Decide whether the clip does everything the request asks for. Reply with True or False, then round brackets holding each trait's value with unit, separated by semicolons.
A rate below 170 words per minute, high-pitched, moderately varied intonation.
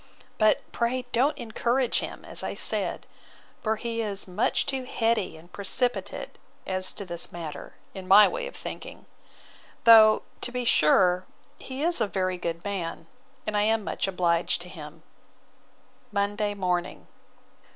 True (150 wpm; 205 Hz; 4.4 semitones)